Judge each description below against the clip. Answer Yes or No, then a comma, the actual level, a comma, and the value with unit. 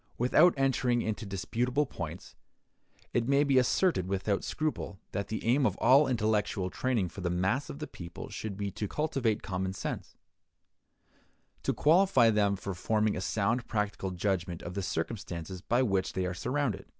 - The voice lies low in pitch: Yes, low, 105 Hz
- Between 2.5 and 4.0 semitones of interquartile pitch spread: No, average, 5.2 semitones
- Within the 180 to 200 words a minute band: No, average, 165 wpm